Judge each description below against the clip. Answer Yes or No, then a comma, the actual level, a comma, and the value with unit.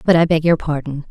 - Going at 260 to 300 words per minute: Yes, fast, 270 wpm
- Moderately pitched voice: Yes, medium, 155 Hz